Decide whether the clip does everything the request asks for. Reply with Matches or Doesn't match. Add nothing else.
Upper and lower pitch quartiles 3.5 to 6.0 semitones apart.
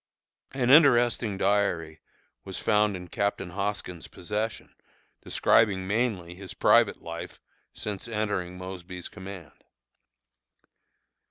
Doesn't match